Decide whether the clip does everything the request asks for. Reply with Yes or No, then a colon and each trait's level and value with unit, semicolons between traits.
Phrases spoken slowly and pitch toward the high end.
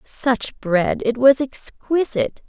Yes: slow, 120 wpm; high, 245 Hz